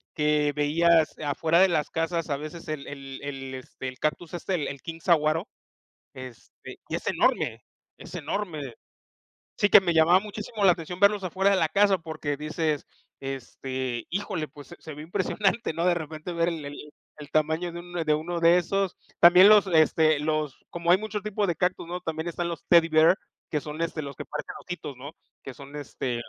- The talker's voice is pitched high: No, medium, 160 Hz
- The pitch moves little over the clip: No, average, 3.1 semitones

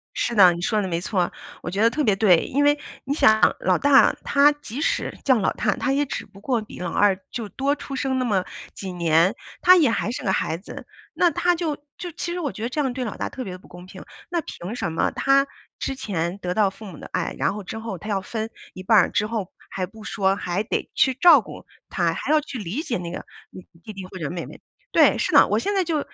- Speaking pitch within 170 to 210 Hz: No, high, 220 Hz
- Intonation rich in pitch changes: Yes, wide, 6.8 semitones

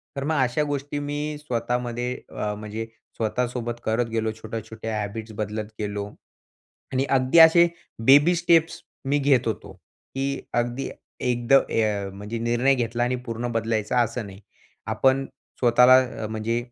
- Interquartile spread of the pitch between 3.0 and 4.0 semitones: Yes, average, 3.3 semitones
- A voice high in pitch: No, low, 120 Hz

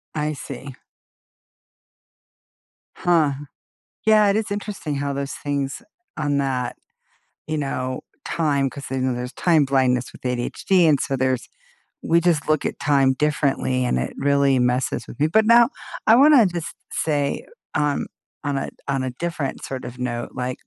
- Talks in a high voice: No, medium, 140 Hz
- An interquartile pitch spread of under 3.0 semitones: No, average, 3.7 semitones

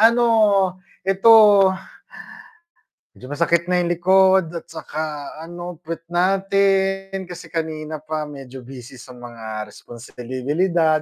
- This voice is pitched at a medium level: Yes, medium, 165 Hz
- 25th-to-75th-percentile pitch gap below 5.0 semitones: No, average, 5.3 semitones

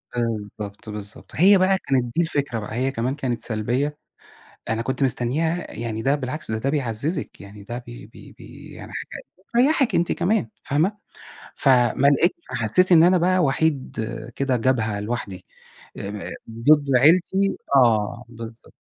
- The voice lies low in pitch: Yes, low, 130 Hz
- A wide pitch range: Yes, wide, 6.1 semitones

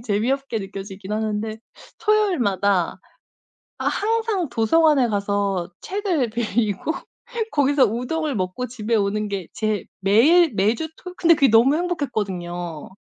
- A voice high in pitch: Yes, high, 225 Hz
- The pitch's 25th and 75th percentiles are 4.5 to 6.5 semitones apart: No, wide, 7.0 semitones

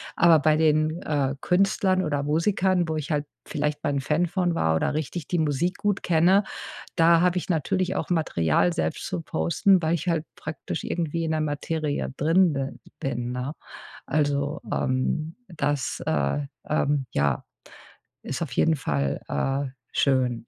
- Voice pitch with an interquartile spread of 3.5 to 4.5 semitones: Yes, average, 3.8 semitones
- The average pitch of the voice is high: No, medium, 155 Hz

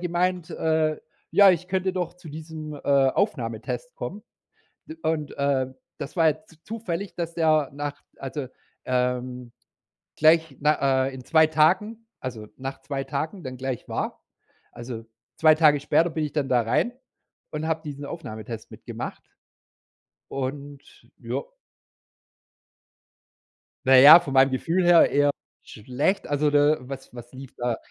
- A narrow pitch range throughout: No, average, 3.7 semitones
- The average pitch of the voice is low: No, medium, 145 Hz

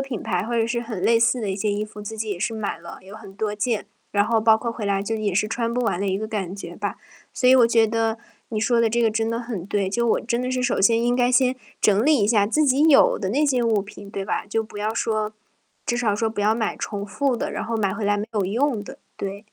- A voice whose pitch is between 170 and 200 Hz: No, high, 220 Hz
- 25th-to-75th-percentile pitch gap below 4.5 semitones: Yes, narrow, 2.5 semitones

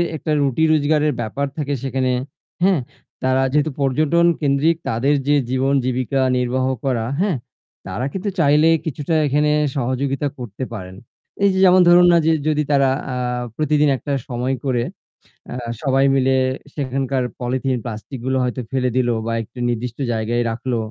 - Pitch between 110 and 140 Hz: Yes, low, 135 Hz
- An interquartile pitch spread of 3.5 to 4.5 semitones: No, average, 3.1 semitones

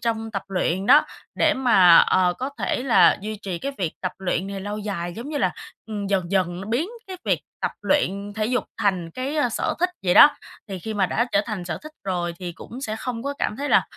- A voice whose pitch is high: Yes, high, 205 Hz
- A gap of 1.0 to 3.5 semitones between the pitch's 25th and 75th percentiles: No, average, 5.1 semitones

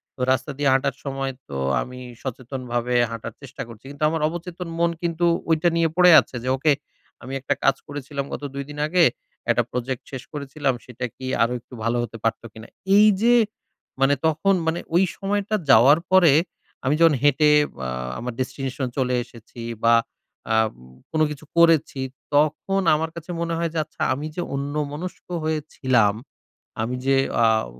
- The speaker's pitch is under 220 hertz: Yes, medium, 140 Hz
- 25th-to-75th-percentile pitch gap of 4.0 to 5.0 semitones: Yes, average, 4.4 semitones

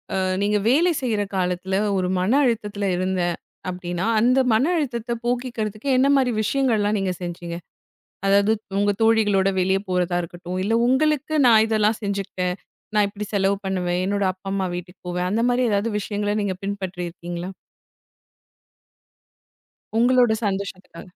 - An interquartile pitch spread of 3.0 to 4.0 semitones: Yes, average, 3.6 semitones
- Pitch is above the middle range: Yes, high, 200 Hz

